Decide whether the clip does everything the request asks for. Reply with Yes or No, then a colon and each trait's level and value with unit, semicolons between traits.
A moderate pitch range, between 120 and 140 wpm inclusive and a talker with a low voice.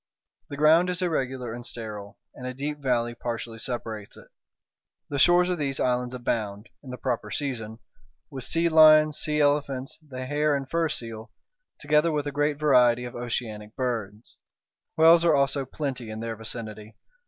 No: average, 4.3 semitones; average, 165 wpm; low, 130 Hz